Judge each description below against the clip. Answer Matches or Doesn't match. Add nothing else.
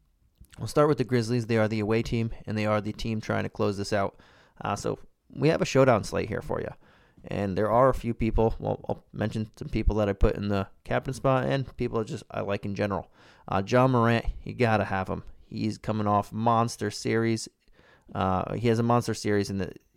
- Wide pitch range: Doesn't match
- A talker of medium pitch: Doesn't match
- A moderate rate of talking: Doesn't match